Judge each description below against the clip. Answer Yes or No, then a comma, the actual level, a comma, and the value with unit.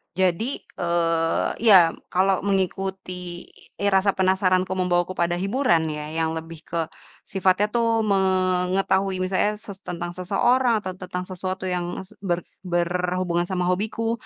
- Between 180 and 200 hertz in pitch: Yes, medium, 185 Hz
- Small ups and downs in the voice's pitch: Yes, narrow, 1.8 semitones